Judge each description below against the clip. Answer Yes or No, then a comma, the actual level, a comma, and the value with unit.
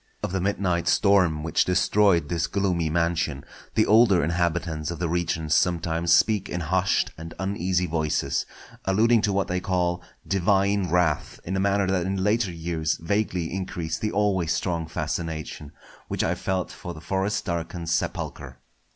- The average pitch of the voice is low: Yes, very low, 90 Hz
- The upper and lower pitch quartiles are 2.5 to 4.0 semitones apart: Yes, average, 2.8 semitones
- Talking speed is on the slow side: No, average, 160 wpm